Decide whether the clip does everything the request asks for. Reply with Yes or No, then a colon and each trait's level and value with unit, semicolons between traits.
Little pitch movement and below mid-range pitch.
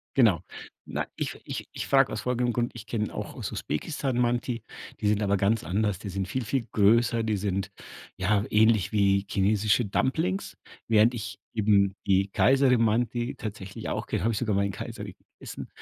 No: average, 3.1 semitones; low, 110 Hz